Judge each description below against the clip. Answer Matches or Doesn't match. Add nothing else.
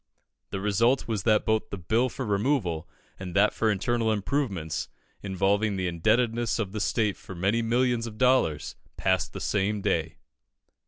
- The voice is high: Doesn't match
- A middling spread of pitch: Matches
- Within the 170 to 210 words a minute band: Doesn't match